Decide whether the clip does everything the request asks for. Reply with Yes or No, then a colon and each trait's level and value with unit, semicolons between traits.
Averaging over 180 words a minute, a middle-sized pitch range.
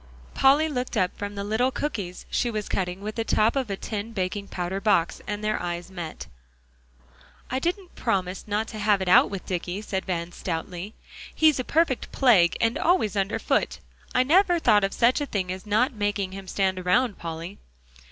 Yes: average, 190 wpm; average, 4.6 semitones